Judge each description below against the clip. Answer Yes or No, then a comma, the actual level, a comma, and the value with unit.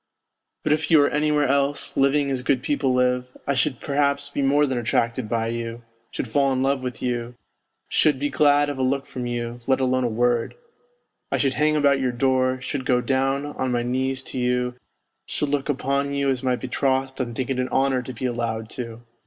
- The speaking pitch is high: No, low, 130 Hz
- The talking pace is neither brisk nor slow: No, fast, 215 wpm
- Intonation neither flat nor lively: No, narrow, 2.2 semitones